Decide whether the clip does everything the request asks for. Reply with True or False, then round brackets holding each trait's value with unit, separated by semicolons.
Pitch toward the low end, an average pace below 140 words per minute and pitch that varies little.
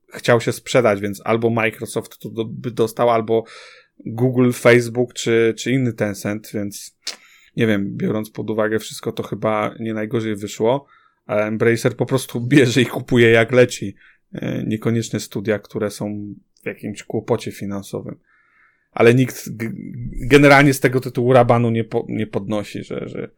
False (115 Hz; 150 wpm; 2.3 semitones)